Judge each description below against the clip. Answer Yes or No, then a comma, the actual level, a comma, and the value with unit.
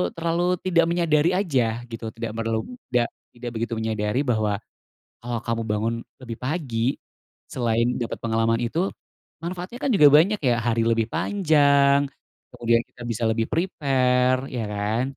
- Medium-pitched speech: No, low, 120 Hz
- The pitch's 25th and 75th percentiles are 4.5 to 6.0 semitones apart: Yes, average, 5.0 semitones